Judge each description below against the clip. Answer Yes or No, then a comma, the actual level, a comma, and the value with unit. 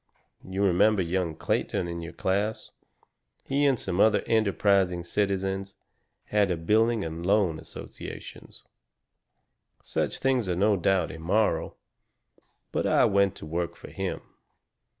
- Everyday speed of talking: No, slow, 130 wpm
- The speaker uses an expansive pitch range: No, average, 3.2 semitones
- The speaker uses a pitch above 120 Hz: No, very low, 95 Hz